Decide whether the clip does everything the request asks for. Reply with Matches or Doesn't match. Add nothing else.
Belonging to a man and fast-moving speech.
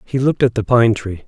Matches